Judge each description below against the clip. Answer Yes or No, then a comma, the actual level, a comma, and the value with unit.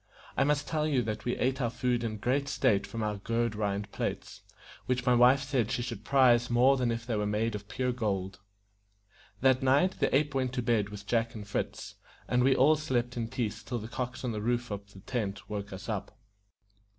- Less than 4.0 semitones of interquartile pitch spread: Yes, average, 3.4 semitones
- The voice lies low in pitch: Yes, low, 120 Hz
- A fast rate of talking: Yes, fast, 220 wpm